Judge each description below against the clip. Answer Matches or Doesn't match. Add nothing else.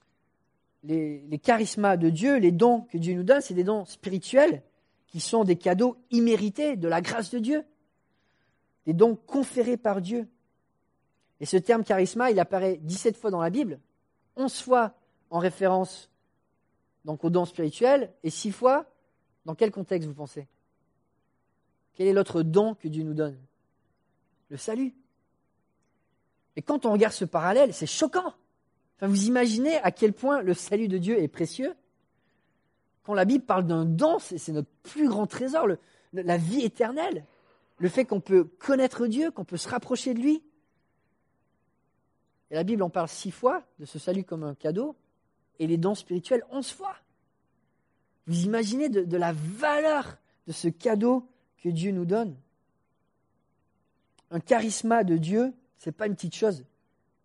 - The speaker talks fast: Doesn't match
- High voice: Matches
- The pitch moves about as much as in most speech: Doesn't match